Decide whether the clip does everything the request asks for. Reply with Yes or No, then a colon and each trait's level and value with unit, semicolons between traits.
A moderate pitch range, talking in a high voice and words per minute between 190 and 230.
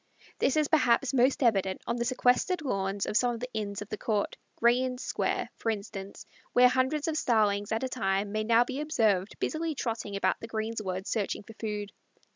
Yes: average, 3.8 semitones; high, 230 Hz; average, 200 wpm